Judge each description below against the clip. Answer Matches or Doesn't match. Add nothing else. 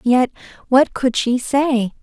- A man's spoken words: Doesn't match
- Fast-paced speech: Doesn't match